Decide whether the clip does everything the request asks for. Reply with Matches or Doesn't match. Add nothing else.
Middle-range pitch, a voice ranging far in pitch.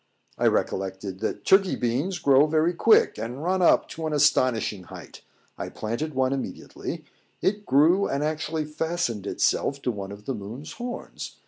Matches